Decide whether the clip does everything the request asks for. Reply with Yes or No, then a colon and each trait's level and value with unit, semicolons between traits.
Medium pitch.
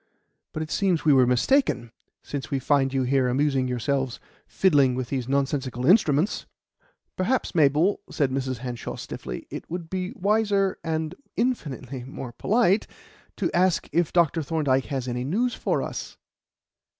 Yes: medium, 145 Hz